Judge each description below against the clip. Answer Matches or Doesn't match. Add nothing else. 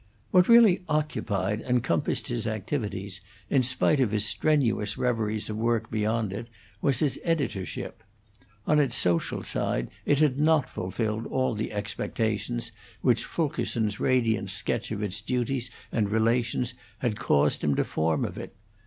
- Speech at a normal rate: Matches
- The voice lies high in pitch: Doesn't match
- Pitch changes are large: Doesn't match